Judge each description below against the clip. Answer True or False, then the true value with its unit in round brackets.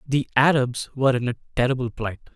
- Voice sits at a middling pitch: False (130 Hz)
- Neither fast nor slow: True (180 wpm)